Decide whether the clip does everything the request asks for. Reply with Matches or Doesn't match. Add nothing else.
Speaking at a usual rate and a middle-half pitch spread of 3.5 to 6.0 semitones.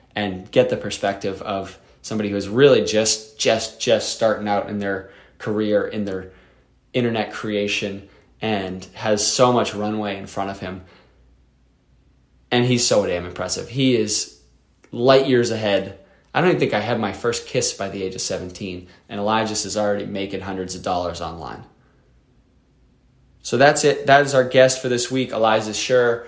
Matches